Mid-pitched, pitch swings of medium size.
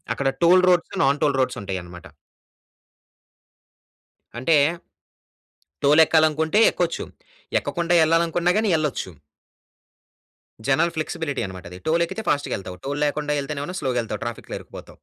Yes: medium, 150 Hz; average, 4.4 semitones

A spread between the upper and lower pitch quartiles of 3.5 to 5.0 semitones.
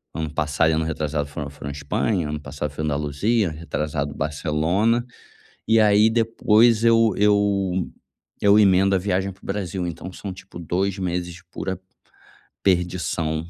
Yes: average, 4.7 semitones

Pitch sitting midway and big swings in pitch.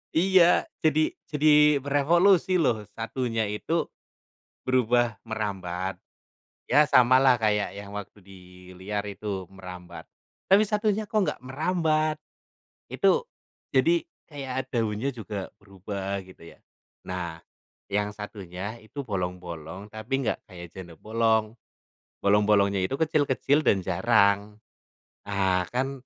No: low, 110 Hz; wide, 6.3 semitones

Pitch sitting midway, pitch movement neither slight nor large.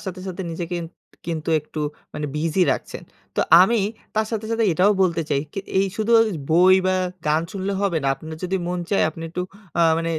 Yes: medium, 180 Hz; average, 3.2 semitones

